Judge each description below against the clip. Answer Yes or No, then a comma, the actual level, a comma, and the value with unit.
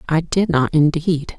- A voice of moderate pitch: Yes, medium, 160 Hz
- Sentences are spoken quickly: No, average, 175 wpm